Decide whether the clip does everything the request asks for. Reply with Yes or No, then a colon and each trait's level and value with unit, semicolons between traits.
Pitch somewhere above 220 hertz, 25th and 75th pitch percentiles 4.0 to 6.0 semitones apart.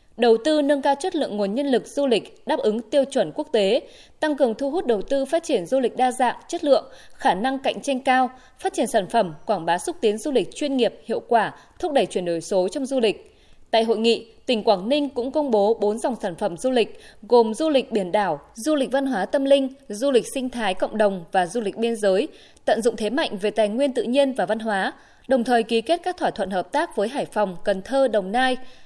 Yes: high, 245 Hz; average, 4.8 semitones